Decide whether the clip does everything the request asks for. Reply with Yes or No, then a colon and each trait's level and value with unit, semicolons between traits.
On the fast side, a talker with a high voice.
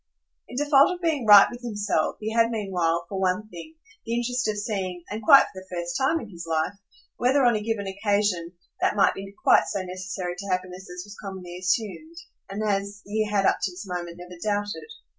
Yes: fast, 210 wpm; high, 200 Hz